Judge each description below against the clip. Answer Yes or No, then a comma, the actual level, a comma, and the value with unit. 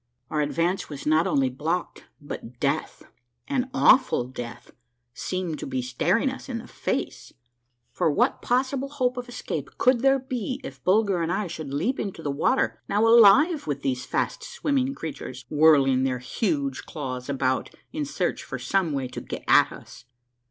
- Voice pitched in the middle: Yes, medium, 170 Hz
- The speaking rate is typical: Yes, average, 170 wpm